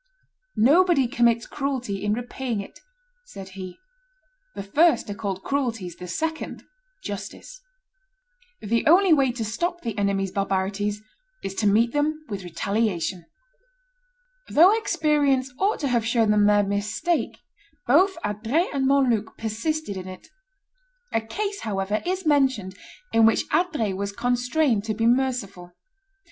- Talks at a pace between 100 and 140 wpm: Yes, slow, 135 wpm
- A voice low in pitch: No, high, 230 Hz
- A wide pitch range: Yes, wide, 6.4 semitones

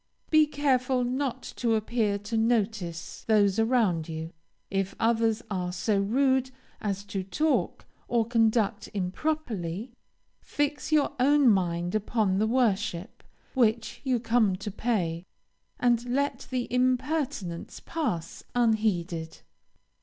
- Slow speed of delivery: Yes, slow, 115 wpm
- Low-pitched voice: No, high, 225 Hz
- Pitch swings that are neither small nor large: Yes, average, 4.5 semitones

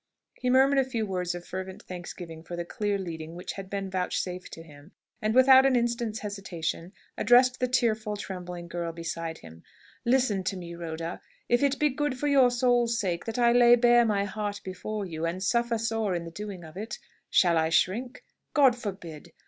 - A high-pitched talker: Yes, high, 200 Hz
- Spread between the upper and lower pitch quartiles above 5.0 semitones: Yes, wide, 5.6 semitones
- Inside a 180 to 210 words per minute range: Yes, average, 195 wpm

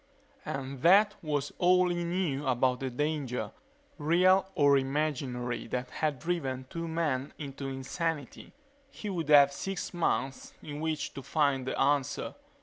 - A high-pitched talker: No, medium, 145 Hz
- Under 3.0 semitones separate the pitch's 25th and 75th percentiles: No, average, 3.9 semitones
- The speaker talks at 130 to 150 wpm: Yes, average, 145 wpm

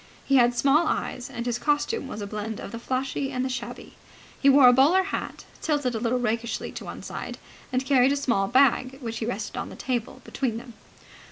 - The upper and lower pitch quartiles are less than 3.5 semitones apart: Yes, narrow, 2.6 semitones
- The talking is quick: Yes, fast, 215 wpm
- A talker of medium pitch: No, very high, 255 Hz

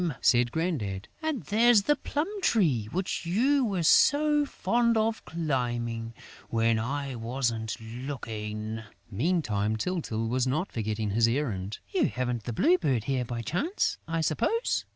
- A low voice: Yes, low, 130 Hz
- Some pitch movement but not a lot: No, wide, 8.5 semitones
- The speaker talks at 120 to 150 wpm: Yes, average, 140 wpm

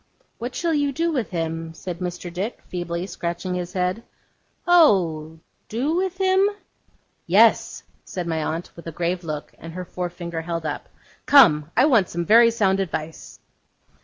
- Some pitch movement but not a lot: No, wide, 5.8 semitones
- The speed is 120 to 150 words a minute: No, average, 160 wpm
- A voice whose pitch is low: No, medium, 180 Hz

